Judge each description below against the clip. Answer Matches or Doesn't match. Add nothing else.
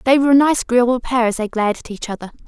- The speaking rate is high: Matches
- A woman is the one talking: Matches